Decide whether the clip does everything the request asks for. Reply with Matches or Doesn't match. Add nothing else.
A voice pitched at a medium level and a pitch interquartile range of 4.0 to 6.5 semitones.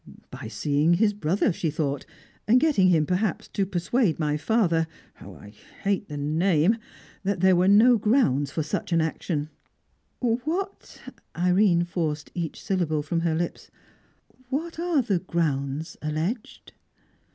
Matches